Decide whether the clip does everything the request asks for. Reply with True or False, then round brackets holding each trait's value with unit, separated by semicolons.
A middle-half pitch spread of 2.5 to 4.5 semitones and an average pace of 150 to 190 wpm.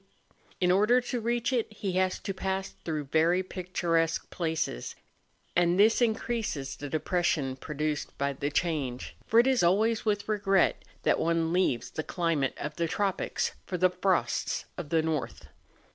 True (4.2 semitones; 160 wpm)